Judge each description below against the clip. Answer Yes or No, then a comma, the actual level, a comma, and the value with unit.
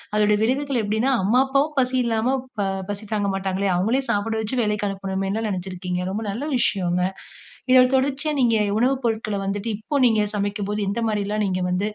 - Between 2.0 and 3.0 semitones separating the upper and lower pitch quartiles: No, average, 3.6 semitones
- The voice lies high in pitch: Yes, high, 210 Hz